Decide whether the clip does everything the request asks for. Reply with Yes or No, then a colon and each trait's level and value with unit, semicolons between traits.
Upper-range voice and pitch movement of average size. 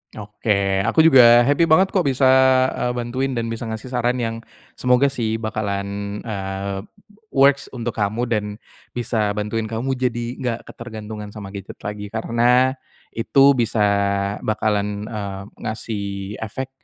No: low, 110 Hz; average, 3.2 semitones